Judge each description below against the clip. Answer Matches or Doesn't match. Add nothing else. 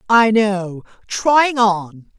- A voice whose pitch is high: Matches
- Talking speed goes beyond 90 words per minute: Doesn't match